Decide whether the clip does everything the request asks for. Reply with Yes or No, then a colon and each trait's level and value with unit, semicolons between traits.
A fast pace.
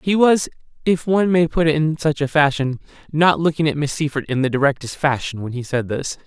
Yes: fast, 230 wpm